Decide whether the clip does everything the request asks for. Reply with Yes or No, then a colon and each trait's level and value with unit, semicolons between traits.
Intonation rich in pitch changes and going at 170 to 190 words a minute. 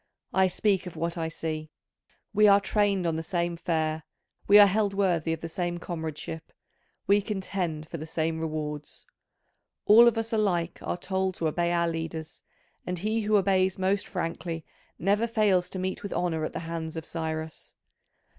No: average, 3.4 semitones; average, 175 wpm